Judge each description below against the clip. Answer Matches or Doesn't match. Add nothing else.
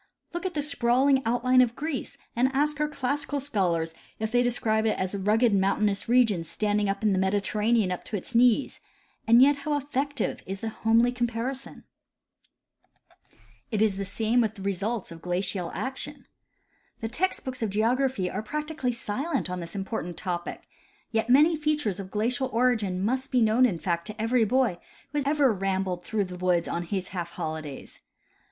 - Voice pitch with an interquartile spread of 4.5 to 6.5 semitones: Matches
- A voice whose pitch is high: Matches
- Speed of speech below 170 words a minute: Doesn't match